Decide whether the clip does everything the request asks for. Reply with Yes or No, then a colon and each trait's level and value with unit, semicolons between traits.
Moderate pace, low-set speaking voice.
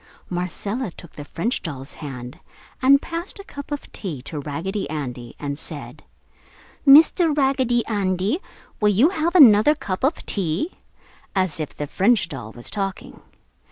No: average, 150 wpm; high, 195 Hz